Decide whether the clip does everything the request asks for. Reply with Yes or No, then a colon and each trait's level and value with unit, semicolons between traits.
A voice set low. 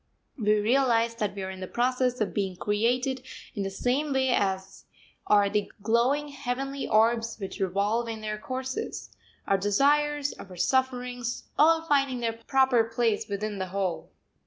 No: high, 230 Hz